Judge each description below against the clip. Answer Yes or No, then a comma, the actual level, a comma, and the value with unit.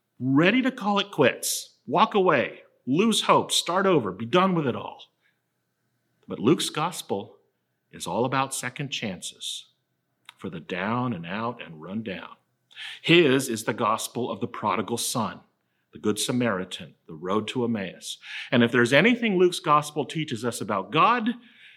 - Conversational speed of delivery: Yes, average, 155 wpm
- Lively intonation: Yes, wide, 8.0 semitones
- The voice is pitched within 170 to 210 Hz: No, low, 135 Hz